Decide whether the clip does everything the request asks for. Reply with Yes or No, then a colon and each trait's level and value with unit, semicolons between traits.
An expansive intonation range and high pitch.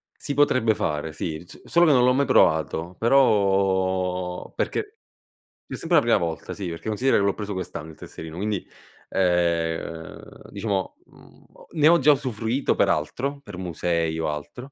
No: wide, 7.2 semitones; very low, 95 Hz